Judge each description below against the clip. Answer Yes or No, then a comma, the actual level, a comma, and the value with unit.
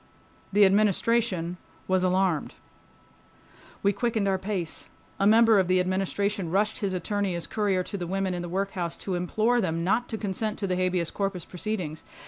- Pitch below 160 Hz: No, high, 190 Hz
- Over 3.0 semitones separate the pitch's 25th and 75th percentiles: No, narrow, 2.4 semitones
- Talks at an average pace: Yes, average, 170 wpm